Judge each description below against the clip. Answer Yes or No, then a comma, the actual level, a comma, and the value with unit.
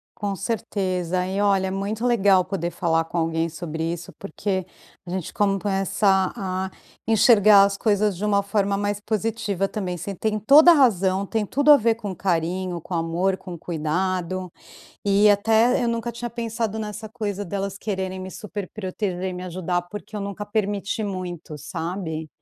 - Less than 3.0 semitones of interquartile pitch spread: Yes, narrow, 2.6 semitones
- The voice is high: Yes, high, 195 Hz